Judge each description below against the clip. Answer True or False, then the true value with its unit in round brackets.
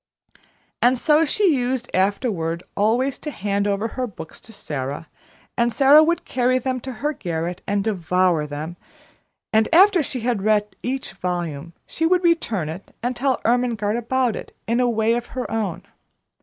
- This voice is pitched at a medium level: False (230 Hz)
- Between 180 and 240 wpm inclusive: False (170 wpm)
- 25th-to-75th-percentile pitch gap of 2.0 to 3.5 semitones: False (5.6 semitones)